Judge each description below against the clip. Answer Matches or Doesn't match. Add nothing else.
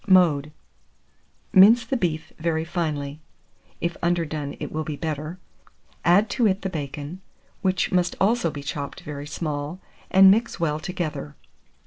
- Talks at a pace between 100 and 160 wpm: Matches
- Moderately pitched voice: Matches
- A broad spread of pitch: Doesn't match